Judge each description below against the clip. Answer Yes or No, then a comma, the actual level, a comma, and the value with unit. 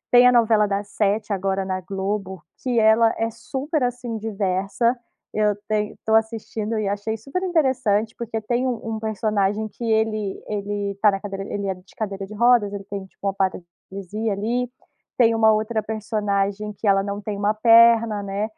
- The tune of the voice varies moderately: No, narrow, 2.2 semitones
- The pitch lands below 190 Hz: No, high, 215 Hz